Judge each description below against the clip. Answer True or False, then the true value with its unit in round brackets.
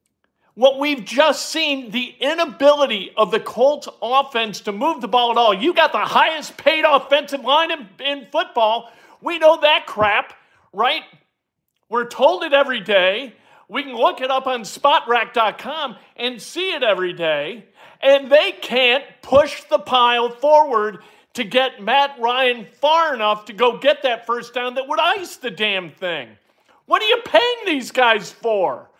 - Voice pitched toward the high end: True (265 Hz)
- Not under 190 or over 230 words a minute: False (165 wpm)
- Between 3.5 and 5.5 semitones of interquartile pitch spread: True (4.3 semitones)